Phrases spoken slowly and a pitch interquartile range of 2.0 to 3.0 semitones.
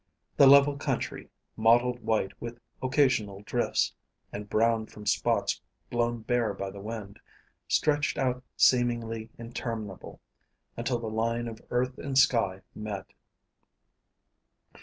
Yes: slow, 115 wpm; narrow, 2.4 semitones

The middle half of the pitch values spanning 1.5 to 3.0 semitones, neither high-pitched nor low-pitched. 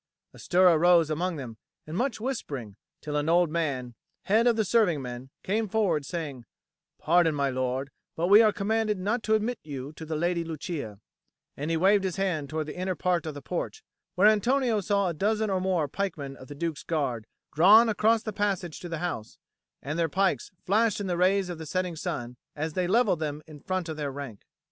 No: average, 5.1 semitones; medium, 175 Hz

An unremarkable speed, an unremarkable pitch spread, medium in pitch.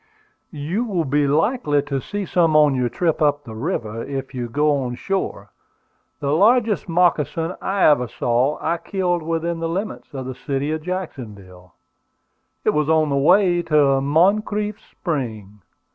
Yes: average, 160 wpm; average, 4.7 semitones; medium, 150 Hz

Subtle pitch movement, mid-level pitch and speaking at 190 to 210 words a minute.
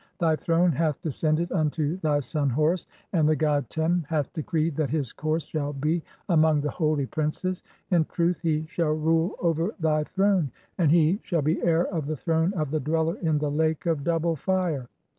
Yes: narrow, 1.8 semitones; medium, 160 Hz; average, 195 wpm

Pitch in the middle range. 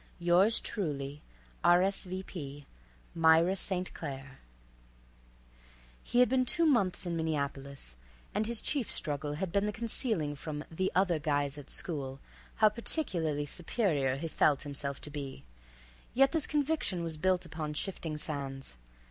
Yes: medium, 165 Hz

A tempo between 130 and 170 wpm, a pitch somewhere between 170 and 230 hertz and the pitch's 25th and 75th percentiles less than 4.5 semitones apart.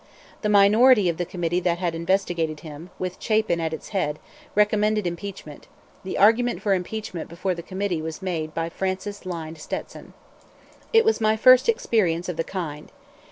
Yes: average, 160 wpm; medium, 185 Hz; average, 4.0 semitones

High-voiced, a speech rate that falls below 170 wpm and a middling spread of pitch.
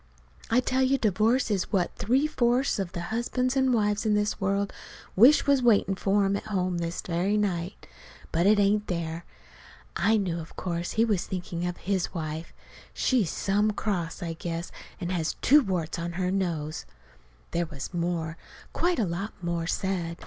No: high, 195 Hz; average, 180 wpm; average, 4.0 semitones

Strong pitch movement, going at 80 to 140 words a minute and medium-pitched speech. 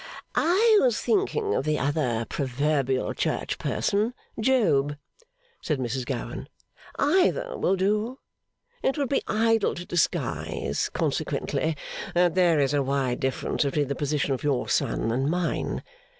Yes: wide, 8.6 semitones; slow, 135 wpm; medium, 155 Hz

